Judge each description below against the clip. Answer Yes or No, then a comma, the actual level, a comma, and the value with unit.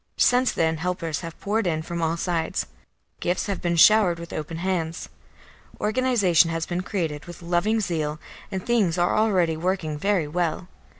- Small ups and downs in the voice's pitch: No, average, 3.2 semitones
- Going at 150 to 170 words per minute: Yes, average, 165 wpm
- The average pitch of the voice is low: No, medium, 175 Hz